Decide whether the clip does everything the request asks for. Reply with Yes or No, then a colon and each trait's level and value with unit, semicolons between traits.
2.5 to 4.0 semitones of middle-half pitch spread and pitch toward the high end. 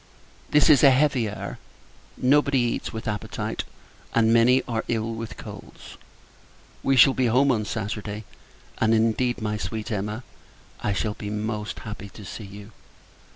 No: average, 3.0 semitones; low, 110 Hz